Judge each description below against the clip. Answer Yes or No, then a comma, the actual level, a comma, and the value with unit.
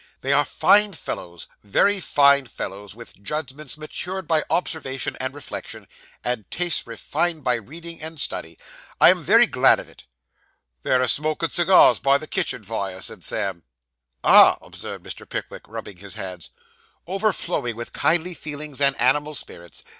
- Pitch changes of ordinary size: No, wide, 6.0 semitones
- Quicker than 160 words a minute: No, average, 155 wpm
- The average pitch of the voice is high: No, medium, 140 Hz